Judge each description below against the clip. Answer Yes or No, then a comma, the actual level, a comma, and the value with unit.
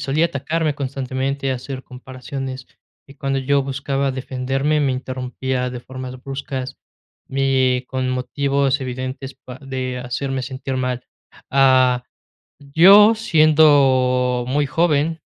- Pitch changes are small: Yes, narrow, 1.5 semitones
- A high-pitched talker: No, low, 135 Hz